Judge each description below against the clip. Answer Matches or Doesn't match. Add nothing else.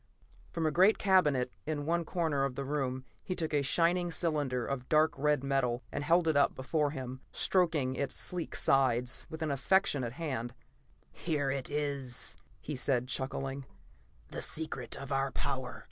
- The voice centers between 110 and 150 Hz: Matches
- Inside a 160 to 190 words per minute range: Matches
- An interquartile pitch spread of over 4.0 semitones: Doesn't match